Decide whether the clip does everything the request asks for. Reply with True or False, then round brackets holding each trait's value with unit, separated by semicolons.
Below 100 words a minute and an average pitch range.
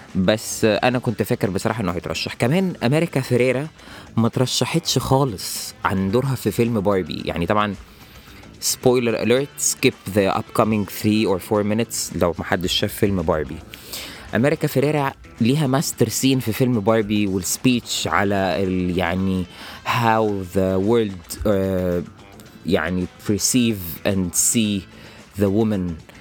False (130 wpm; 4.1 semitones)